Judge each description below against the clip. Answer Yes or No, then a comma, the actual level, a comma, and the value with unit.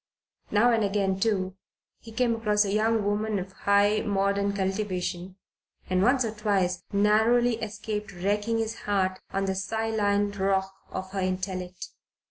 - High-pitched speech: Yes, high, 205 Hz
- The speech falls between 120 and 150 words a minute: Yes, average, 145 wpm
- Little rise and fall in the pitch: Yes, narrow, 2.2 semitones